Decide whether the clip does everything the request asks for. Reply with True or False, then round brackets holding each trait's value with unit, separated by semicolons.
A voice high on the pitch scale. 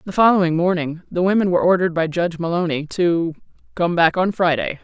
False (175 Hz)